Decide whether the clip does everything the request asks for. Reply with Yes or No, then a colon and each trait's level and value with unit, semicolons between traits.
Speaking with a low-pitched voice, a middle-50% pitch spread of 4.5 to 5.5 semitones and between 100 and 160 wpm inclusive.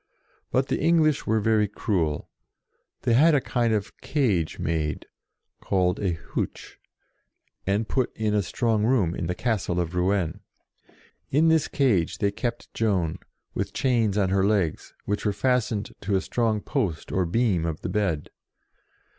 Yes: low, 105 Hz; average, 4.9 semitones; average, 155 wpm